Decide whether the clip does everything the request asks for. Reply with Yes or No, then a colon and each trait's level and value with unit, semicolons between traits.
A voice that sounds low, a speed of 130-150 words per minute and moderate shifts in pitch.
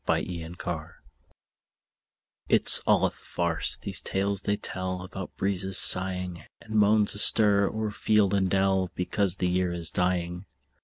No: very low, 95 Hz; average, 145 wpm; narrow, 2.1 semitones